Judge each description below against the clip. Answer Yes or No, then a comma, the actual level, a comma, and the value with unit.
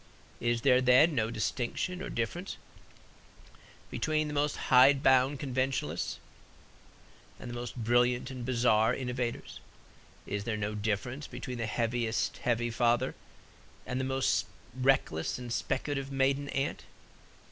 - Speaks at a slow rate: Yes, slow, 125 wpm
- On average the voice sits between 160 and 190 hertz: No, low, 125 Hz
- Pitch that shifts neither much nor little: No, narrow, 2.3 semitones